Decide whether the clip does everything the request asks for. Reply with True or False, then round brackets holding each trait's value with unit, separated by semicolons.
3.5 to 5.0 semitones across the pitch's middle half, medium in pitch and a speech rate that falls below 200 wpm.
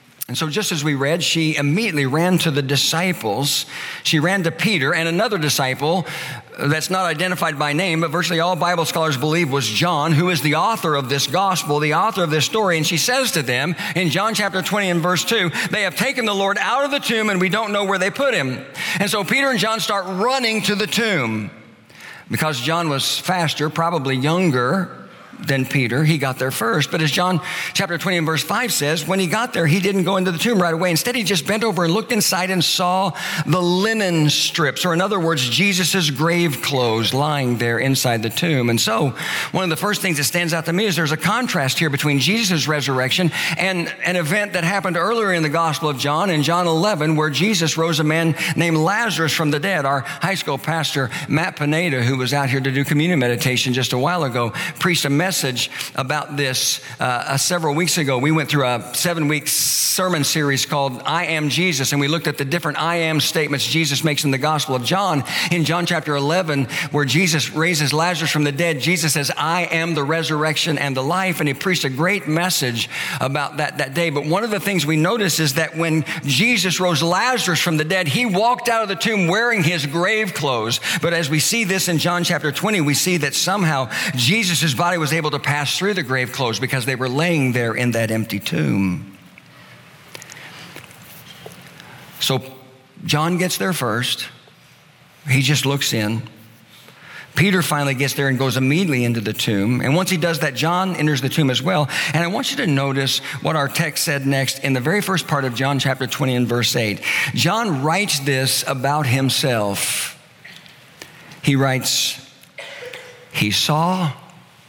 False (4.5 semitones; 160 Hz; 205 wpm)